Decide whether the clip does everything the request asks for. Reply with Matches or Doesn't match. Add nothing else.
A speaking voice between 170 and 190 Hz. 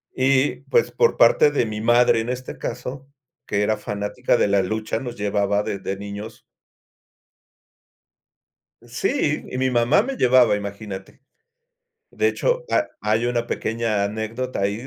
Doesn't match